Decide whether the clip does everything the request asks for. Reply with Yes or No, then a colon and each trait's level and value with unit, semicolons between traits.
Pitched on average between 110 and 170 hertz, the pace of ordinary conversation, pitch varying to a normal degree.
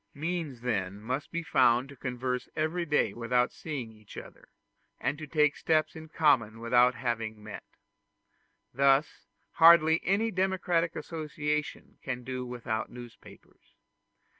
No: low, 135 Hz; slow, 130 wpm; average, 4.7 semitones